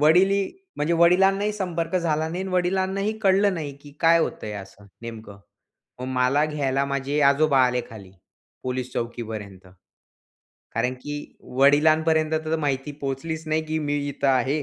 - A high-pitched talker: No, medium, 150 Hz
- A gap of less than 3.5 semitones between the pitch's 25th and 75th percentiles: No, average, 4.5 semitones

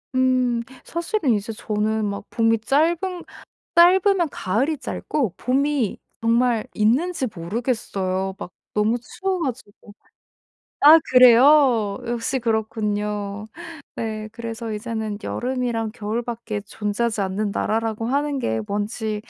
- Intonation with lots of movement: No, average, 3.6 semitones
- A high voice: Yes, high, 230 Hz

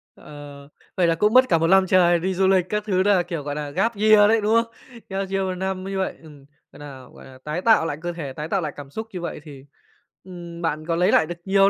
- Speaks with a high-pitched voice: No, medium, 175 Hz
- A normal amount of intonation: Yes, average, 4.1 semitones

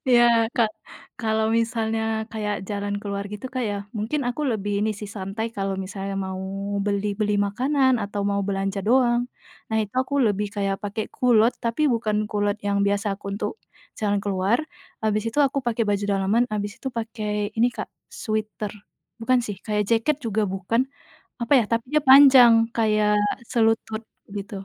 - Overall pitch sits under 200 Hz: No, high, 215 Hz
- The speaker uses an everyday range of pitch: No, narrow, 2.2 semitones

